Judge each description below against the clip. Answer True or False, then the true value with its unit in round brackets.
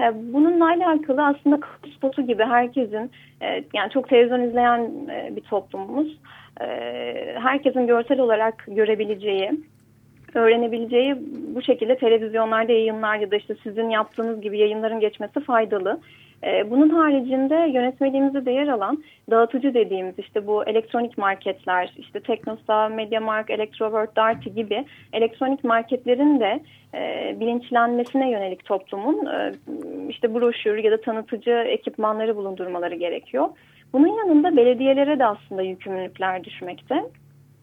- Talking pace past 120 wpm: False (110 wpm)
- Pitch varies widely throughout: False (3.6 semitones)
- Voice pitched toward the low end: False (230 Hz)